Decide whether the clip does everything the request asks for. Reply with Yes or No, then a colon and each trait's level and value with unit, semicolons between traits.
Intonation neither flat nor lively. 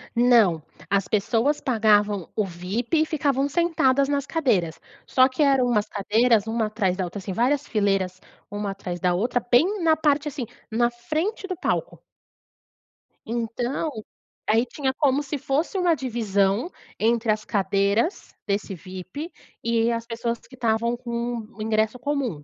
Yes: average, 5.0 semitones